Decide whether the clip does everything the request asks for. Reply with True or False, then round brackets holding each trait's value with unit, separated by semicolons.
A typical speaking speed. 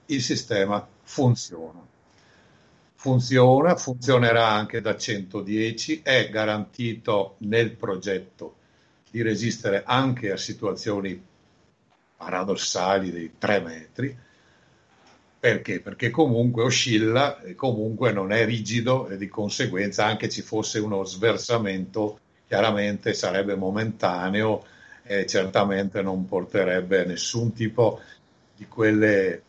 False (100 wpm)